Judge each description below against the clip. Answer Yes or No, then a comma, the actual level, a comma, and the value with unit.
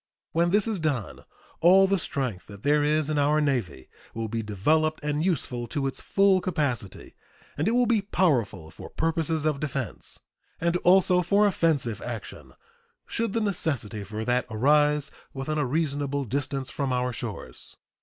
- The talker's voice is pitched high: No, medium, 145 Hz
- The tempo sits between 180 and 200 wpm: No, average, 165 wpm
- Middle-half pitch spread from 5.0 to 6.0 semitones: Yes, average, 5.3 semitones